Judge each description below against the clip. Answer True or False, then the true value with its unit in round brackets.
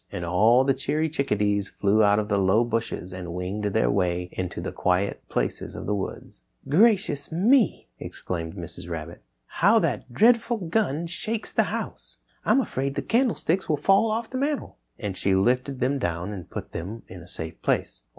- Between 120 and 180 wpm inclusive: False (190 wpm)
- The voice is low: True (110 Hz)